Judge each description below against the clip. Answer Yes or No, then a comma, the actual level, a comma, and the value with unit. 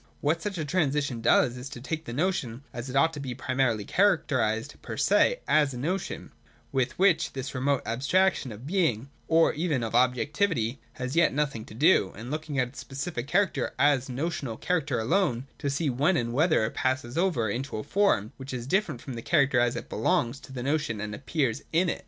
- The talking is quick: Yes, fast, 210 wpm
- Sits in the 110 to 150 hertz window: Yes, low, 135 Hz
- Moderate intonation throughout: Yes, average, 4.7 semitones